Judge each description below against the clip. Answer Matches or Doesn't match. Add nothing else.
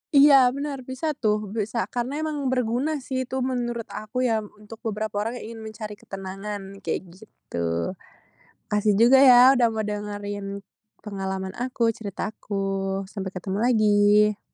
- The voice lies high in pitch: Matches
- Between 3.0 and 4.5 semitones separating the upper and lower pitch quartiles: Matches